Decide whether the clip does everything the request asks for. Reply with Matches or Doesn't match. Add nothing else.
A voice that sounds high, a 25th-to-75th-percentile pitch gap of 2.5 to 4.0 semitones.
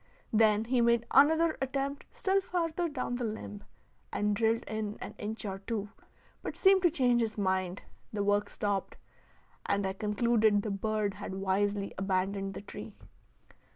Matches